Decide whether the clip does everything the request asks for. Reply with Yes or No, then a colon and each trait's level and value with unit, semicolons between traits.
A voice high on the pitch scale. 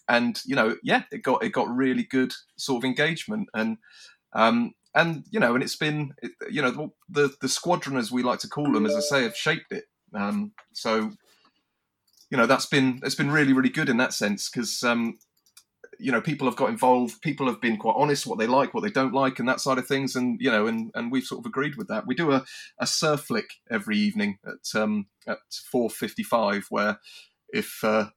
No: low, 130 Hz